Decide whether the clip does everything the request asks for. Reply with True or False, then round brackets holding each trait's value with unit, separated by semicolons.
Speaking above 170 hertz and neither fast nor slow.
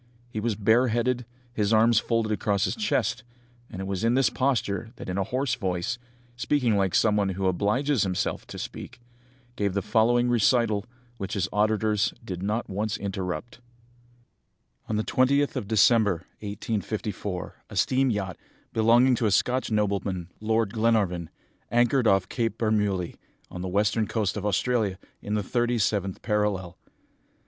False (110 Hz; 155 wpm)